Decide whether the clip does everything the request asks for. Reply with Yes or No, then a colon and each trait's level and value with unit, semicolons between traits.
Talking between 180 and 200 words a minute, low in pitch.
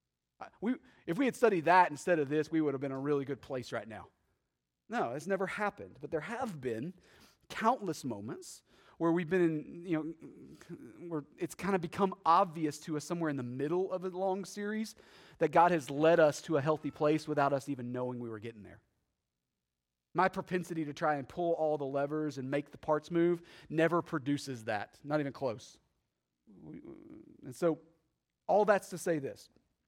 No: average, 195 wpm; medium, 155 Hz